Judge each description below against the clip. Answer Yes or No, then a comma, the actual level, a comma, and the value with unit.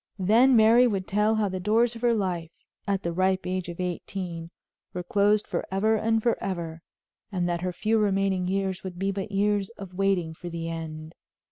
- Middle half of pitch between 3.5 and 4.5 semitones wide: No, average, 2.9 semitones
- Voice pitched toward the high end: Yes, high, 195 Hz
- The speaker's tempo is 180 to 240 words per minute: Yes, average, 190 wpm